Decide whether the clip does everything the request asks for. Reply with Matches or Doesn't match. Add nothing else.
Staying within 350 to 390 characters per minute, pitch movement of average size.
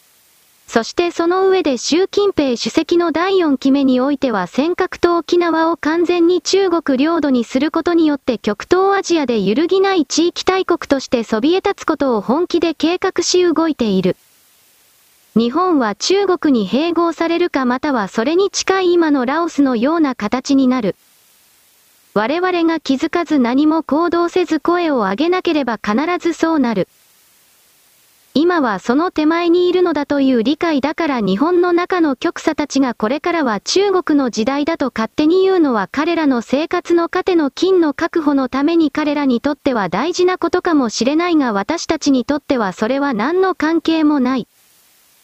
Doesn't match